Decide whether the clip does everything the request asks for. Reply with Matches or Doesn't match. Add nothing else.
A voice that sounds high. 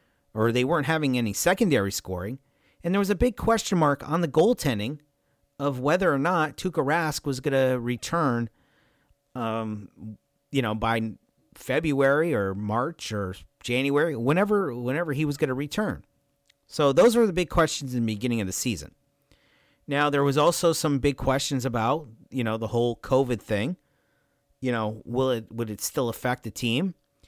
Doesn't match